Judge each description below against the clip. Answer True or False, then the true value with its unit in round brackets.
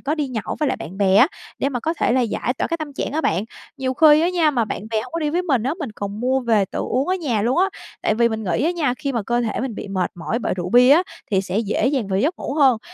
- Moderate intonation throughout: False (5.7 semitones)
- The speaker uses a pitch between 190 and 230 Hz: False (250 Hz)